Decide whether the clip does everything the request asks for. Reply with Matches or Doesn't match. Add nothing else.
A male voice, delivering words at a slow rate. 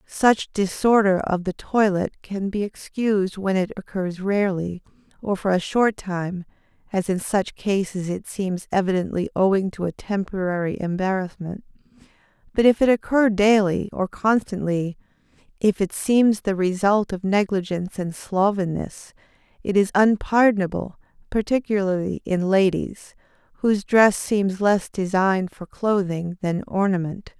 Doesn't match